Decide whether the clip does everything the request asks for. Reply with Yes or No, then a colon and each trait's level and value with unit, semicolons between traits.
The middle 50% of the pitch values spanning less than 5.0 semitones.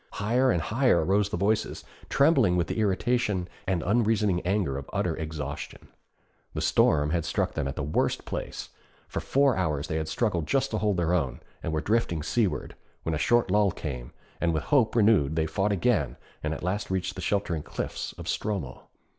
No: average, 5.3 semitones